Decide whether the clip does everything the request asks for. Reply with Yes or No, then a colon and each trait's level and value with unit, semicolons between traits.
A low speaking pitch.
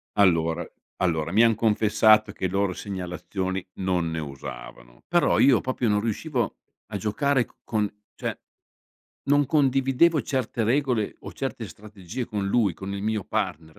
Yes: low, 105 Hz